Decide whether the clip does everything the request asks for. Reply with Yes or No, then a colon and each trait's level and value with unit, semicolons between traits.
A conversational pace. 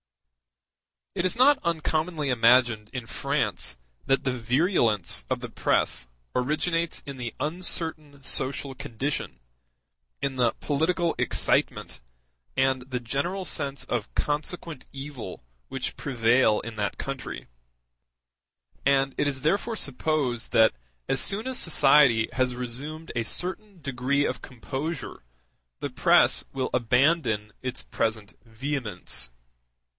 No: slow, 120 wpm